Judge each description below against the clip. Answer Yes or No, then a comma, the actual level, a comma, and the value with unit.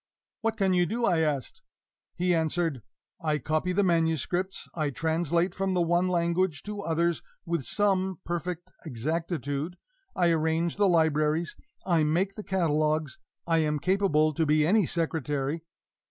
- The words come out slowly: No, average, 145 wpm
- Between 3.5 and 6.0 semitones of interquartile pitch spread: No, average, 2.8 semitones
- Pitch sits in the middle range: Yes, medium, 170 Hz